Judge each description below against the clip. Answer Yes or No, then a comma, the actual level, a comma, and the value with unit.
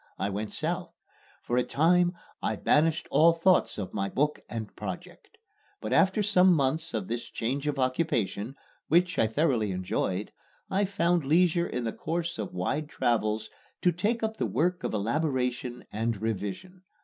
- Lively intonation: Yes, wide, 7.7 semitones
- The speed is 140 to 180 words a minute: Yes, average, 160 wpm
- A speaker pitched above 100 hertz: Yes, medium, 140 Hz